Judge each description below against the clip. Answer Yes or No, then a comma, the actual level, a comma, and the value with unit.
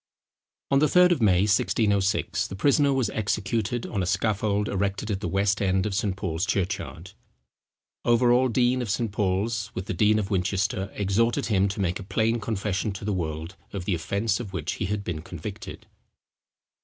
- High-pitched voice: No, low, 100 Hz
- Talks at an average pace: Yes, average, 185 wpm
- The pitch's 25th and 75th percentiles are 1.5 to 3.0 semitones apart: Yes, average, 2.7 semitones